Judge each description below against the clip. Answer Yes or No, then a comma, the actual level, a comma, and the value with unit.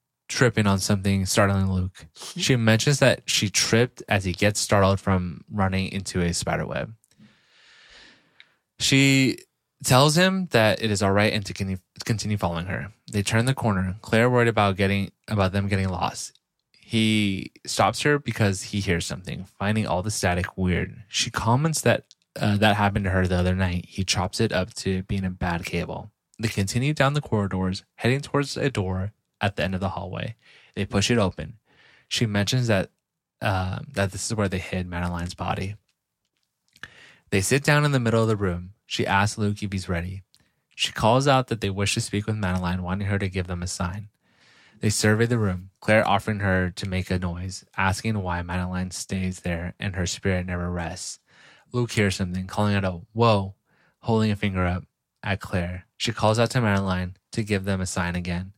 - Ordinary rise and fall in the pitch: Yes, average, 3.2 semitones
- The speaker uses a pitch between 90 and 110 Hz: Yes, low, 100 Hz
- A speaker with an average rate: Yes, average, 190 wpm